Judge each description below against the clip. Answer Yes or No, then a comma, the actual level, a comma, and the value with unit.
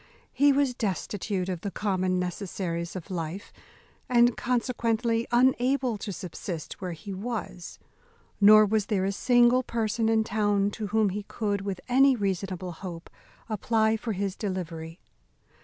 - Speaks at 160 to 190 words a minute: No, average, 140 wpm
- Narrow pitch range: No, average, 3.7 semitones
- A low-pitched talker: No, high, 205 Hz